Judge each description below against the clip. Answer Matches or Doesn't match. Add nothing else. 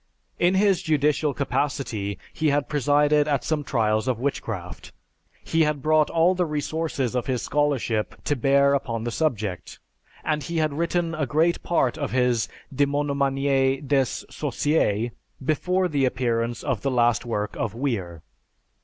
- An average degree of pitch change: Matches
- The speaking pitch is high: Doesn't match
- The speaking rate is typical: Matches